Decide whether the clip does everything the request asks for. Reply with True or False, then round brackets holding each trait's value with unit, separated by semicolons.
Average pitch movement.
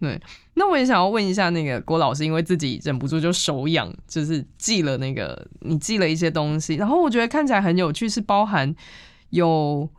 True (4.8 semitones)